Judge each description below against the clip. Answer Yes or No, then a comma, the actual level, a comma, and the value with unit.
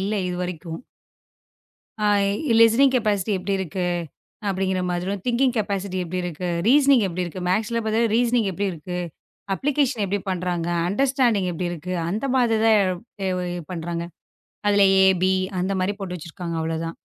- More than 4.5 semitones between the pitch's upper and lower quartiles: No, average, 4.1 semitones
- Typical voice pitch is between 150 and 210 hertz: Yes, high, 190 Hz